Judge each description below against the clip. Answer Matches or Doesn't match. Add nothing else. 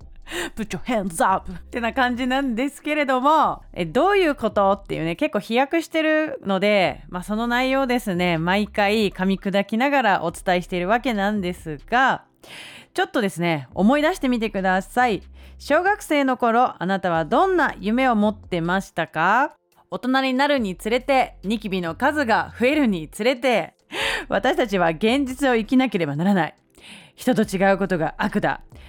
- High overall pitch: Matches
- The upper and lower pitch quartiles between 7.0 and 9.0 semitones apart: Doesn't match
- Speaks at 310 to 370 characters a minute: Matches